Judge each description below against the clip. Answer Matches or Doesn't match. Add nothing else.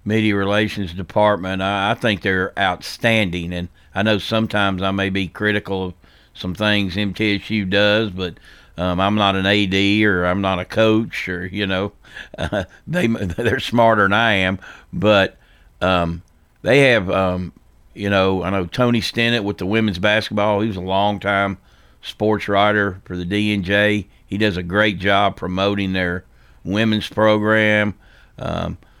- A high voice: Doesn't match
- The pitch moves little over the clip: Matches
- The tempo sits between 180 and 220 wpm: Doesn't match